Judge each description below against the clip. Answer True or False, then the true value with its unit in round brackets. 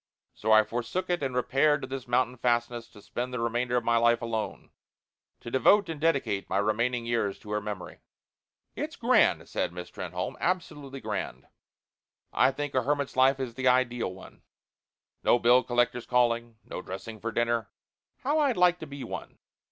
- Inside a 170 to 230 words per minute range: True (175 wpm)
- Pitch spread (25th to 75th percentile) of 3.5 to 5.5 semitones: False (2.8 semitones)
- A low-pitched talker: True (120 Hz)